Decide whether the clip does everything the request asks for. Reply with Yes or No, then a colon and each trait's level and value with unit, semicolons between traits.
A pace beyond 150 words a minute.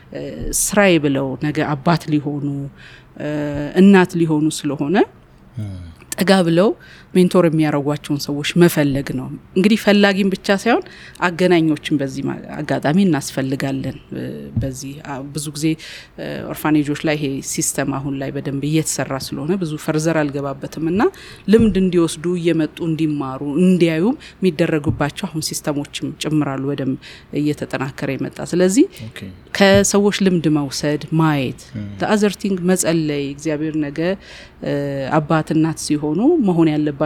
No: slow, 105 wpm